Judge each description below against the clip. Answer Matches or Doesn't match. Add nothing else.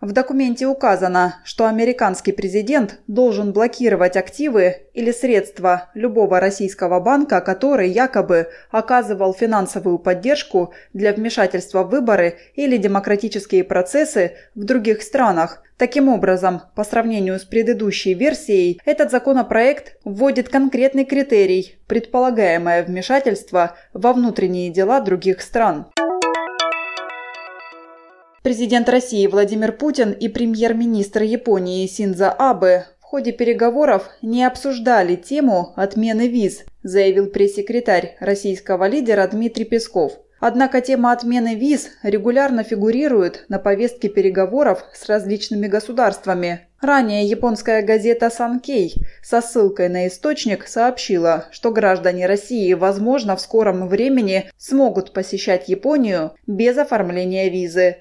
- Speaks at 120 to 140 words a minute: Doesn't match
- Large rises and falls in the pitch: Doesn't match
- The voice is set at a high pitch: Matches